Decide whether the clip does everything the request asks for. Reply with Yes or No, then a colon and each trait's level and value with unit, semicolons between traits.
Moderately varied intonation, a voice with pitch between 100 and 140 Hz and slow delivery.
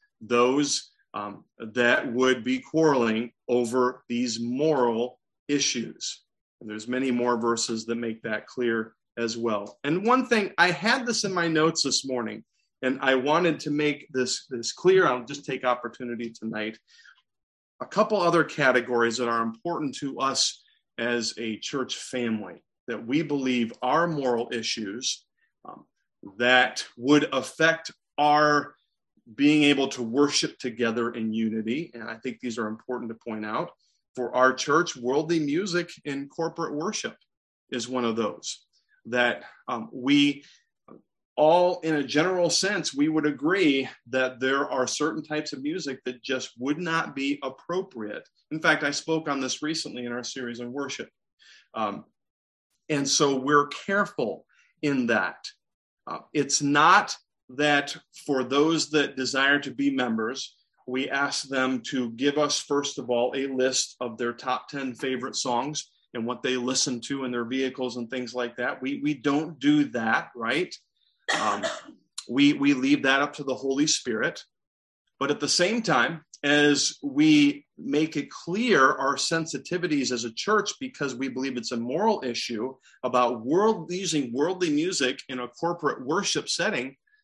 No: average, 4.0 semitones; low, 135 Hz; average, 155 wpm